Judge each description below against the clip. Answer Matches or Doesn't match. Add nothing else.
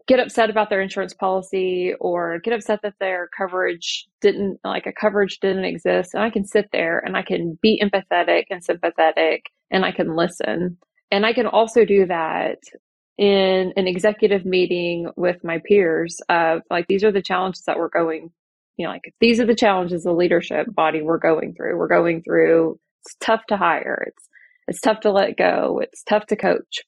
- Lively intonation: Doesn't match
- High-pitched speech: Matches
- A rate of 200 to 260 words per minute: Doesn't match